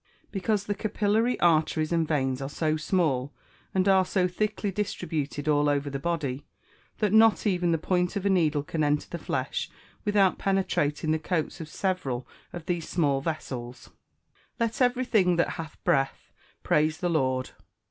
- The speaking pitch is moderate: Yes, medium, 165 Hz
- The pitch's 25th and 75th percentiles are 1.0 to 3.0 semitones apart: No, average, 4.7 semitones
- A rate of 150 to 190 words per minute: Yes, average, 170 wpm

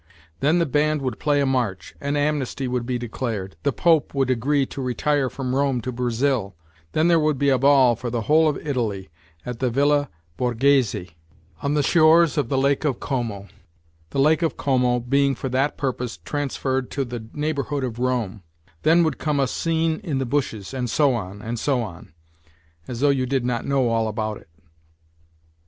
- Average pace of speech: Yes, average, 190 wpm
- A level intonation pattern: No, average, 3.3 semitones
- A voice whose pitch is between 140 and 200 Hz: No, low, 130 Hz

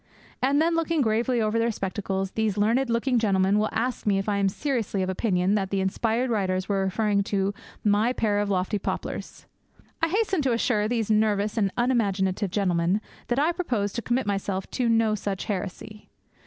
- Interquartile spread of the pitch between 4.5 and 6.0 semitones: No, average, 3.4 semitones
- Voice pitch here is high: Yes, high, 210 Hz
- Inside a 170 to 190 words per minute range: Yes, average, 185 wpm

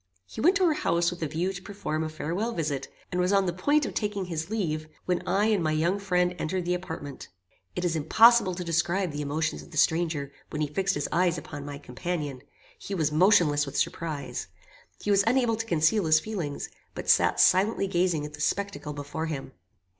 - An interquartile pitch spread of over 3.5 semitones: Yes, average, 4.2 semitones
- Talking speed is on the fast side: Yes, fast, 210 wpm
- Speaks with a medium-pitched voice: Yes, medium, 175 Hz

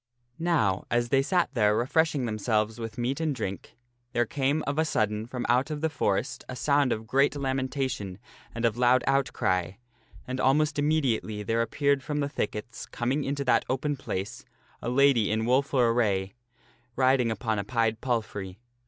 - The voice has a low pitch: Yes, low, 125 Hz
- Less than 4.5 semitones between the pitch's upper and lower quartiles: Yes, average, 4.0 semitones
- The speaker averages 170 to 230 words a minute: Yes, average, 175 wpm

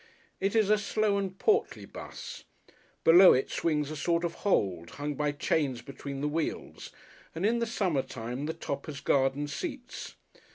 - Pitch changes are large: Yes, wide, 6.2 semitones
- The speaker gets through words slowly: No, average, 170 wpm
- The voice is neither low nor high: Yes, medium, 155 Hz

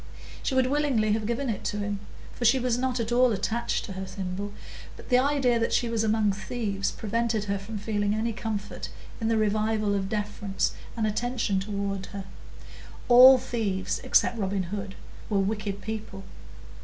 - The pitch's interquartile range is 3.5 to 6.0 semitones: No, average, 2.8 semitones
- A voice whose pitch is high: Yes, high, 215 Hz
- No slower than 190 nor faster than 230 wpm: No, average, 175 wpm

